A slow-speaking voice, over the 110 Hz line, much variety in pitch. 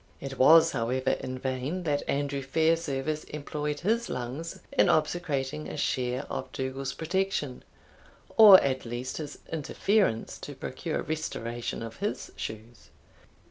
No: slow, 130 wpm; medium, 140 Hz; average, 3.9 semitones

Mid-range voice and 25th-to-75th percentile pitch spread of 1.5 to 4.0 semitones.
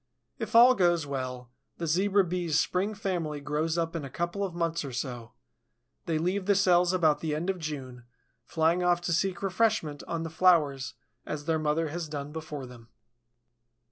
Yes: medium, 165 Hz; average, 3.5 semitones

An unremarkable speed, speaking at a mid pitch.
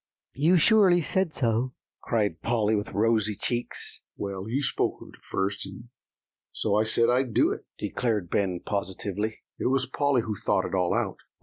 No: average, 175 wpm; low, 110 Hz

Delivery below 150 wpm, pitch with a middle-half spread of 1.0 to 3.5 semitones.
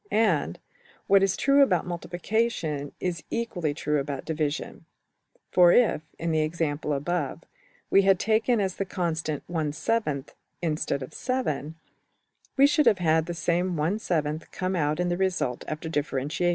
No: average, 140 wpm; average, 4.0 semitones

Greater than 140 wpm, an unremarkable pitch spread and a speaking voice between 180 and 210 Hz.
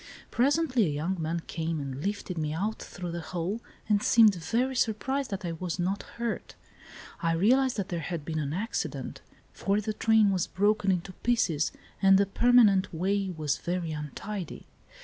Yes: average, 170 wpm; average, 4.6 semitones; high, 190 Hz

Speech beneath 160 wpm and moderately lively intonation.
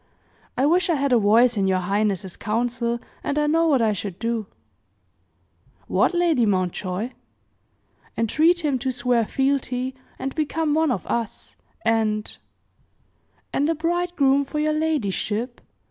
No: average, 145 wpm; wide, 5.8 semitones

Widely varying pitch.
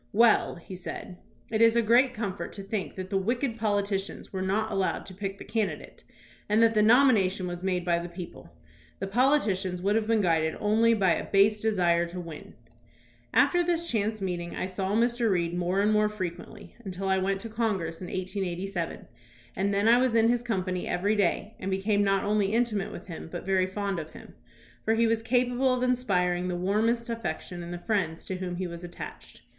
No: average, 3.5 semitones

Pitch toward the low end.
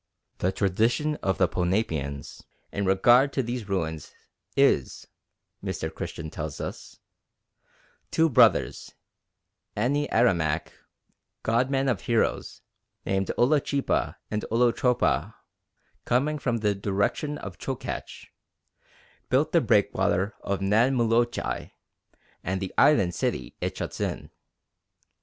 Yes: low, 110 Hz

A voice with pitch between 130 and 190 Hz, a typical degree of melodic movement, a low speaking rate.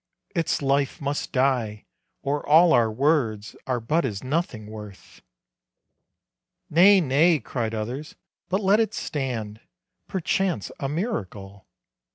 No: low, 135 Hz; wide, 6.8 semitones; slow, 120 wpm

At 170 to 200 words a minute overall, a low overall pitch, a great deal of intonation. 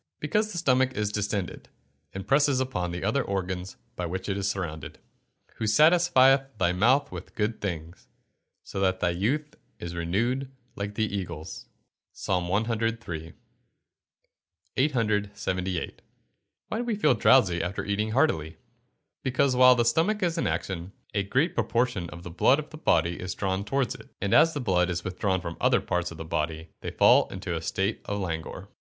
Yes: average, 175 wpm; low, 100 Hz; wide, 6.6 semitones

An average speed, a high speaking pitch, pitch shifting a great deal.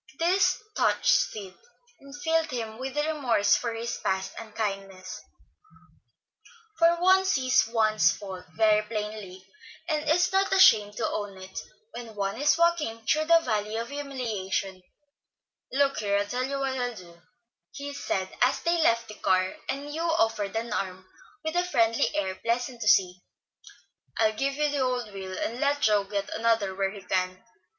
Yes: average, 160 wpm; high, 225 Hz; wide, 6.1 semitones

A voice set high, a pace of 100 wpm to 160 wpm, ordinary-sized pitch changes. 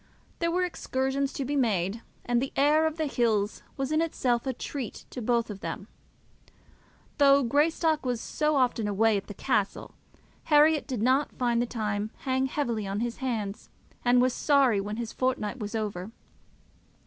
No: high, 245 Hz; average, 170 wpm; average, 4.4 semitones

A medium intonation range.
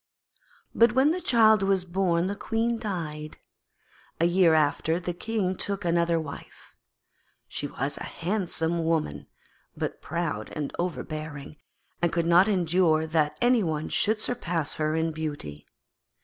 Yes: average, 3.8 semitones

